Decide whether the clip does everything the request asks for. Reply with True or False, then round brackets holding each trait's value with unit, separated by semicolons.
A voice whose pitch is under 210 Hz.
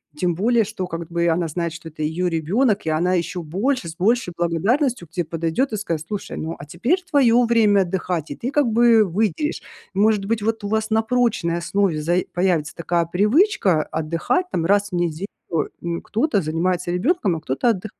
True (185 Hz)